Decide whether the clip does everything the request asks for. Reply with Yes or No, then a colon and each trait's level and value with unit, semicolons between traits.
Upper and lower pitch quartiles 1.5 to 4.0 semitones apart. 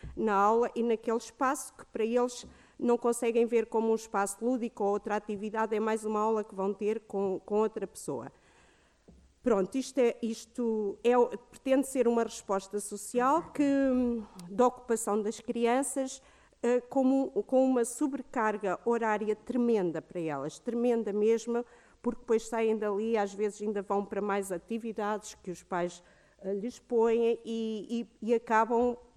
Yes: narrow, 2.5 semitones